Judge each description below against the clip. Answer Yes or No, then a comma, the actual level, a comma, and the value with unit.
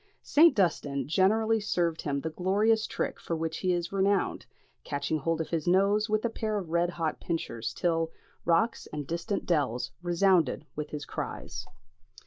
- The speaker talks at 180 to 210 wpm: No, average, 165 wpm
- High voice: No, medium, 170 Hz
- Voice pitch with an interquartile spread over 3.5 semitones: Yes, average, 3.9 semitones